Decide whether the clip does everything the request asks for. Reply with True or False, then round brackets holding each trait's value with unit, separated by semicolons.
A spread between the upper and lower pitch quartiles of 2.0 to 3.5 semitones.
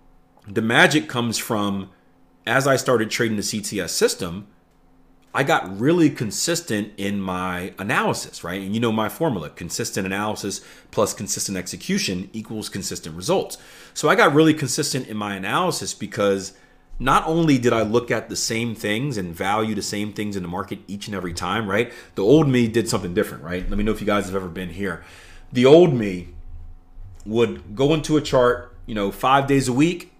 False (4.7 semitones)